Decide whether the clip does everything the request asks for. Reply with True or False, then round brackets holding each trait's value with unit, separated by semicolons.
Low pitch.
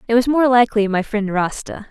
False (225 Hz)